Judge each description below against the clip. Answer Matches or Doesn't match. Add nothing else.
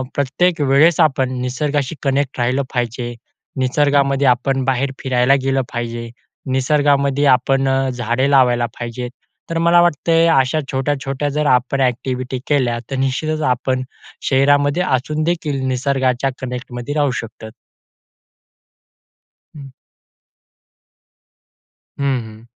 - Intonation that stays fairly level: Matches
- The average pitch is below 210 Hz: Matches